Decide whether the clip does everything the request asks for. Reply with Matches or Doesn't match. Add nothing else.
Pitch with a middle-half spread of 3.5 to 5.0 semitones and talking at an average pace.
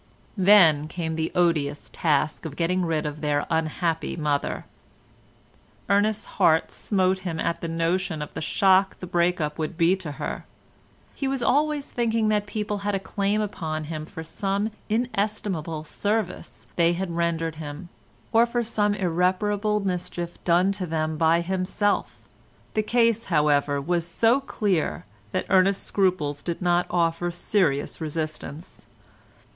Matches